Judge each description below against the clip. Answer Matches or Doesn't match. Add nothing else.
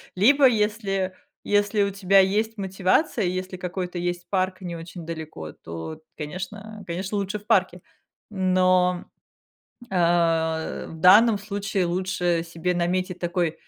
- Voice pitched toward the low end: Doesn't match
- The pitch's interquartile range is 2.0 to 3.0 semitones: Matches